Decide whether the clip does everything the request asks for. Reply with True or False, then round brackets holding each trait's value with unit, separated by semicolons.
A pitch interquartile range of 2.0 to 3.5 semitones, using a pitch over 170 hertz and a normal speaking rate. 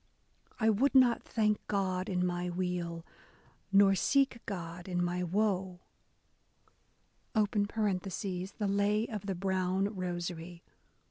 False (2.6 semitones; 190 Hz; 110 wpm)